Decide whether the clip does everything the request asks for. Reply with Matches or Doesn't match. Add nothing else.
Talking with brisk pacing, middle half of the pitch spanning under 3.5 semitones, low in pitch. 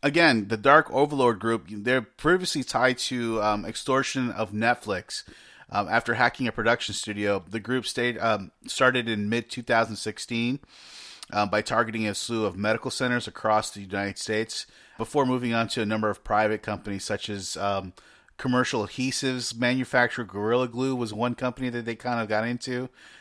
Doesn't match